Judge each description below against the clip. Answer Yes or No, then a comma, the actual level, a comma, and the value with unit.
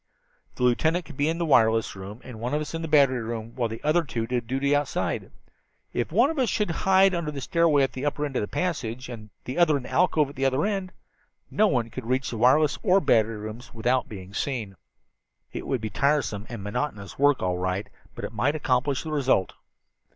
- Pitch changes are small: No, average, 5.1 semitones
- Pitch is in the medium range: No, low, 130 Hz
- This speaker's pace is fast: Yes, fast, 225 wpm